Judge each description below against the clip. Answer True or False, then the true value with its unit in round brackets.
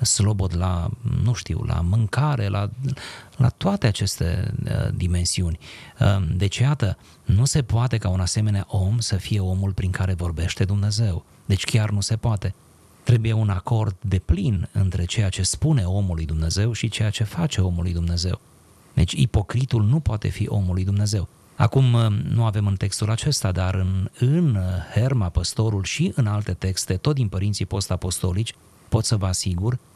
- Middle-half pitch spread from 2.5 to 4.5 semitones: True (3.7 semitones)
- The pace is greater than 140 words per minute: True (165 wpm)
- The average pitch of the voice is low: True (105 Hz)